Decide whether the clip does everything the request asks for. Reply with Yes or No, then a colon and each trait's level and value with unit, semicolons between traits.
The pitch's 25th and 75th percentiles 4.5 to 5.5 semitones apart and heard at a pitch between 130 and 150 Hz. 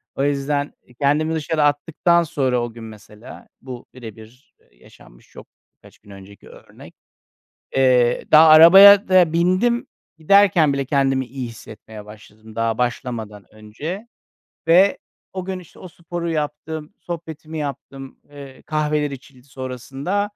Yes: average, 5.1 semitones; medium, 140 Hz